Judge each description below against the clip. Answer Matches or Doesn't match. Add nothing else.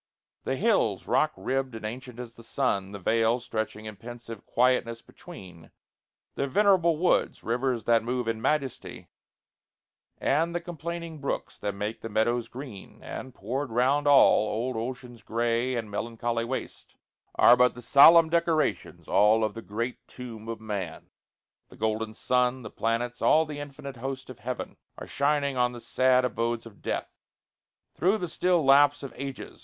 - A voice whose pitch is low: Matches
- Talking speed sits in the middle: Matches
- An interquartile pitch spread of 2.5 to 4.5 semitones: Matches